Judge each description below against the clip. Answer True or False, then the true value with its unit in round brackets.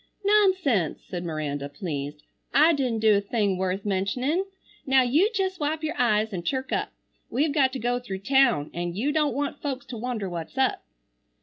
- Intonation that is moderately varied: False (7.2 semitones)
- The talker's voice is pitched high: True (245 Hz)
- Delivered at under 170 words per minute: False (185 wpm)